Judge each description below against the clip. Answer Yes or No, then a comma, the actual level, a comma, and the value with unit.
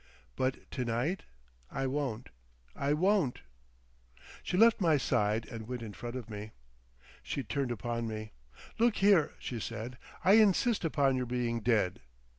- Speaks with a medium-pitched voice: No, low, 125 Hz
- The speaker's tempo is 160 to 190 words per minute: No, average, 140 wpm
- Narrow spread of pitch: No, average, 5.2 semitones